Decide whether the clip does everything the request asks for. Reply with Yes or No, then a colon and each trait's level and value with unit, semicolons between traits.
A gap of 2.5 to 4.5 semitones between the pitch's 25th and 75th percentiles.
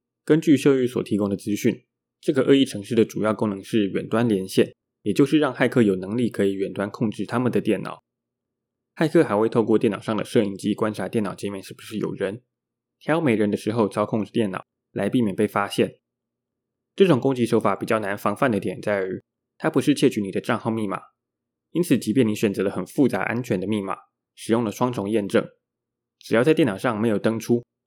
Yes: average, 2.9 semitones